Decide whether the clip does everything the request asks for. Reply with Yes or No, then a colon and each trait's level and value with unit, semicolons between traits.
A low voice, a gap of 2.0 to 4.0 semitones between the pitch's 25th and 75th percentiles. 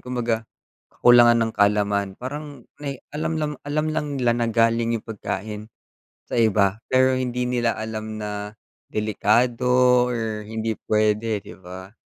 Yes: low, 115 Hz; average, 2.8 semitones